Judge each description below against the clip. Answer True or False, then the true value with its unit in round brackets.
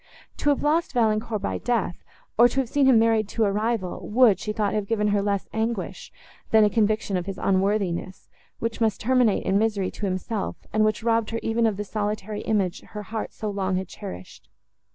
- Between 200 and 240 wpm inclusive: True (205 wpm)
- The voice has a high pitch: True (215 Hz)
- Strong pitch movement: False (2.4 semitones)